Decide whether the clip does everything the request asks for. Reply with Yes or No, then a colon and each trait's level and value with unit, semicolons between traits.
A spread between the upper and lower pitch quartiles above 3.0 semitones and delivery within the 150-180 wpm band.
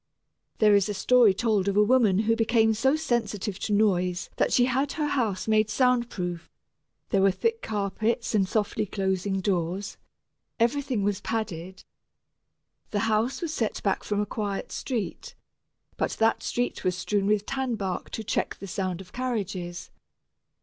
Yes: average, 3.5 semitones; average, 160 wpm